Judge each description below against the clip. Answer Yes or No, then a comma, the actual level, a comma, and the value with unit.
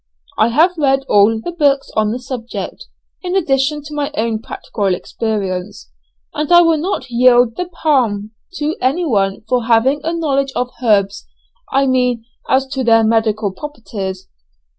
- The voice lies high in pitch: Yes, very high, 250 Hz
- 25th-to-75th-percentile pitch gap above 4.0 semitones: Yes, average, 5.1 semitones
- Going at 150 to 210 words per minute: Yes, average, 155 wpm